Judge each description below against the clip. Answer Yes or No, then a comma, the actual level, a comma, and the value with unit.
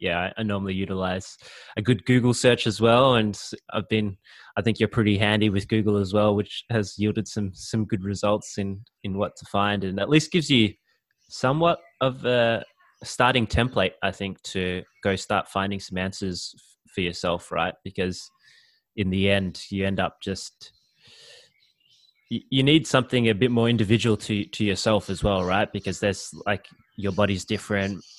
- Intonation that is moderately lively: Yes, average, 3.0 semitones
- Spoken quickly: No, average, 175 wpm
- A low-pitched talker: Yes, low, 105 Hz